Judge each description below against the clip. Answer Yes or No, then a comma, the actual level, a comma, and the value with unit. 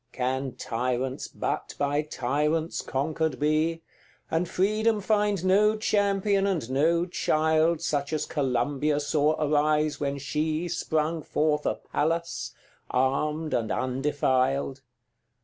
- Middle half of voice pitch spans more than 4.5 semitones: No, average, 3.2 semitones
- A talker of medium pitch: Yes, medium, 150 Hz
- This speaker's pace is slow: Yes, slow, 115 wpm